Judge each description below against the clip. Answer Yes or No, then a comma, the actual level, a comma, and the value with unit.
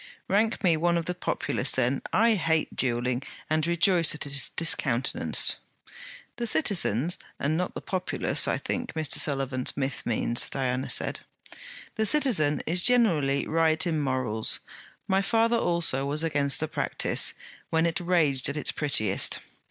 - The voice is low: No, medium, 155 Hz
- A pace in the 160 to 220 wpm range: No, average, 150 wpm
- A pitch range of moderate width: Yes, average, 4.7 semitones